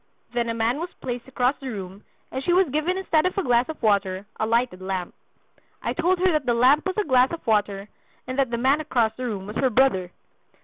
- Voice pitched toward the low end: No, very high, 250 Hz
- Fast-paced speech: Yes, fast, 235 wpm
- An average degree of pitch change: No, wide, 5.8 semitones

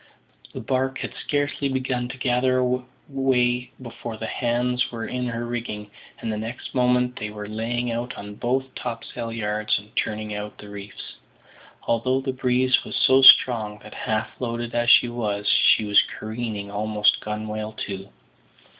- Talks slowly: No, average, 155 wpm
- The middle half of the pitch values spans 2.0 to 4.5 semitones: Yes, average, 2.8 semitones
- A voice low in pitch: Yes, low, 120 Hz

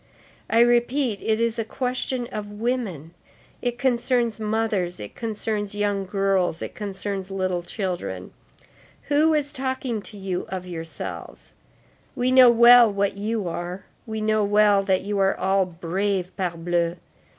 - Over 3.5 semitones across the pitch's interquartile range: Yes, average, 4.0 semitones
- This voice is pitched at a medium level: No, high, 205 Hz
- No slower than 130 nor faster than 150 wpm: Yes, average, 140 wpm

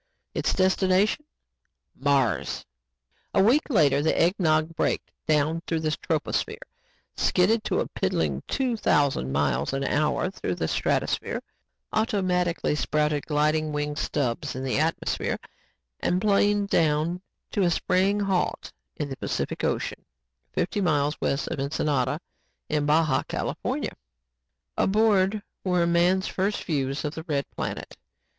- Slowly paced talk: Yes, slow, 130 wpm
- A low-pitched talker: No, medium, 160 Hz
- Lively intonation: No, average, 4.3 semitones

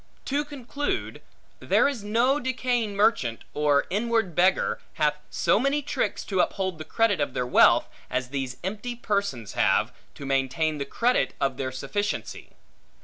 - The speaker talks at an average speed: Yes, average, 150 wpm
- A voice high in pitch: Yes, high, 200 Hz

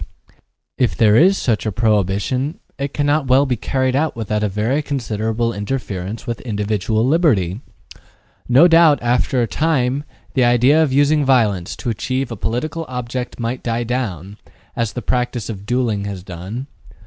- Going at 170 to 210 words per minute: No, average, 160 wpm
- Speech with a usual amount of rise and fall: Yes, average, 4.1 semitones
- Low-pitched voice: Yes, low, 120 Hz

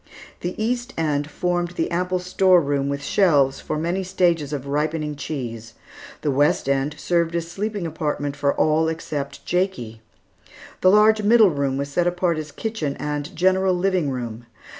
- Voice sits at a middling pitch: Yes, medium, 160 Hz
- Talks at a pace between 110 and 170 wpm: Yes, average, 160 wpm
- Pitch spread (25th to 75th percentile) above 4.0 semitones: Yes, average, 4.4 semitones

